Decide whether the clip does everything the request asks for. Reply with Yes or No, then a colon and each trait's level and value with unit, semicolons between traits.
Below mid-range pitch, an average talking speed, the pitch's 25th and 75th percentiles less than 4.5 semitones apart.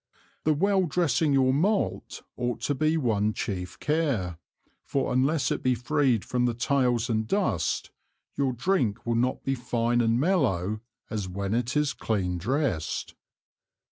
No: low, 125 Hz; average, 150 wpm; average, 4.9 semitones